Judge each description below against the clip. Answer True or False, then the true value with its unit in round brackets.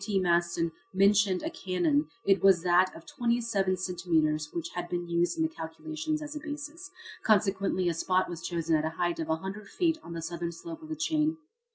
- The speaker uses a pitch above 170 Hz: True (185 Hz)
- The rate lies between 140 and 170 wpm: False (205 wpm)